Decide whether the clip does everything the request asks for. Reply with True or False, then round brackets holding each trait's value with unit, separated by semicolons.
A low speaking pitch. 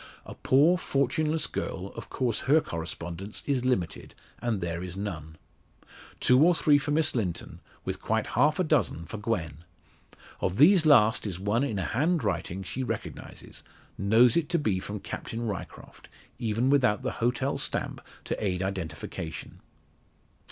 True (115 Hz)